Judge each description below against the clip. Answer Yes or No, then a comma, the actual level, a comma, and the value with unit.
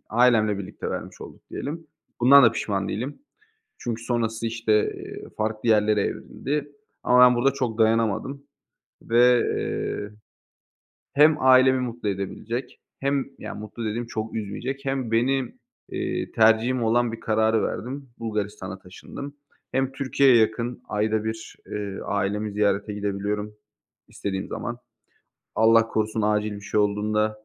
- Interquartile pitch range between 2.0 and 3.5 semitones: Yes, average, 2.9 semitones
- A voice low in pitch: Yes, low, 110 Hz